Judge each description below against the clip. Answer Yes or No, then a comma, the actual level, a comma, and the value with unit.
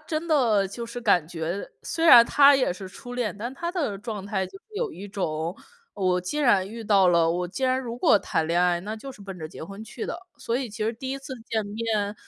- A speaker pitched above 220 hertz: No, high, 215 Hz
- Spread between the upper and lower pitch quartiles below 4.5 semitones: No, average, 5.1 semitones